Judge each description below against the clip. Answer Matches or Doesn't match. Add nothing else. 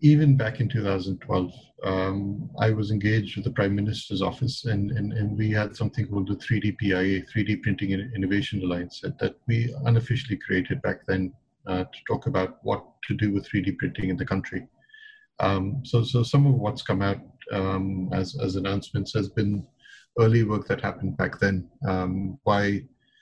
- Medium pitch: Doesn't match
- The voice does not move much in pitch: Doesn't match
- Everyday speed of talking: Matches